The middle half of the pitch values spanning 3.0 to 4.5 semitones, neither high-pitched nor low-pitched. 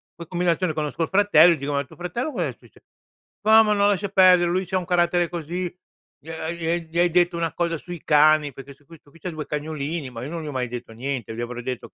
Yes: average, 3.5 semitones; medium, 165 Hz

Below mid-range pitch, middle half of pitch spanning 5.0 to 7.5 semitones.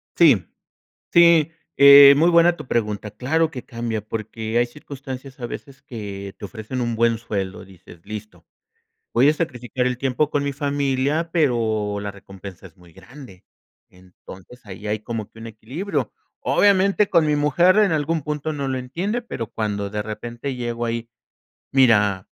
Yes: low, 120 Hz; wide, 5.5 semitones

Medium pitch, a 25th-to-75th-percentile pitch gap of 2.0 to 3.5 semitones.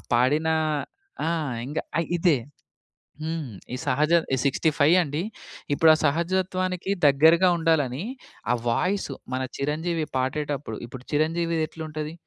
Yes: medium, 155 Hz; average, 2.8 semitones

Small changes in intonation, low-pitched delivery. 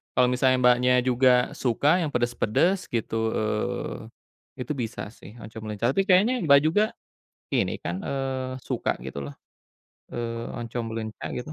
No: average, 3.4 semitones; low, 125 Hz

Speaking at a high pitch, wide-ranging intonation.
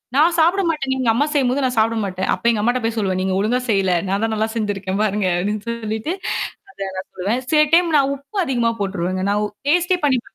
Yes: high, 225 Hz; wide, 5.8 semitones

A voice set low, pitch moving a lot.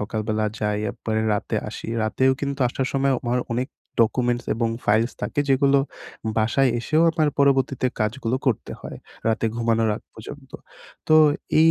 No: low, 120 Hz; average, 3.7 semitones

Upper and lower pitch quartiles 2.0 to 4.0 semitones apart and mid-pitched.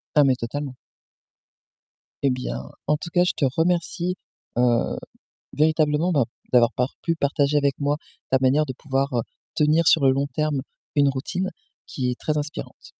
Yes: average, 2.8 semitones; medium, 145 Hz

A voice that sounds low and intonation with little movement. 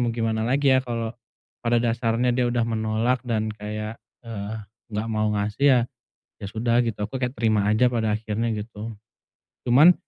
Yes: low, 115 Hz; narrow, 1.9 semitones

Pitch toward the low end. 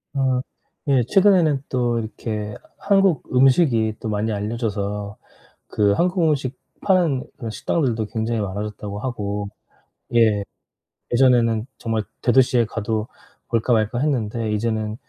Yes: low, 115 Hz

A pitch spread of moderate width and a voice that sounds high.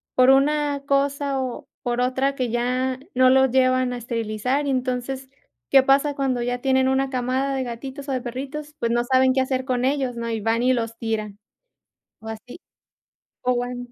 No: narrow, 1.8 semitones; very high, 255 Hz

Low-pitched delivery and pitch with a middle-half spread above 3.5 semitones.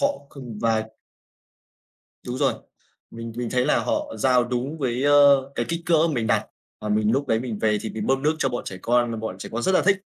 Yes: low, 125 Hz; average, 4.0 semitones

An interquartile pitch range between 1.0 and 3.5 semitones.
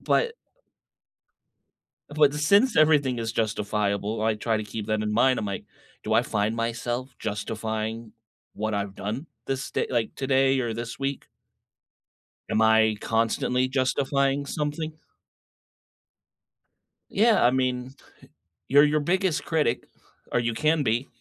No: average, 4.2 semitones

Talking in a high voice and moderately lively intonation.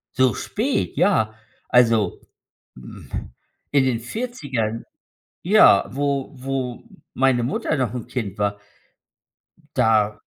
No: low, 125 Hz; average, 4.0 semitones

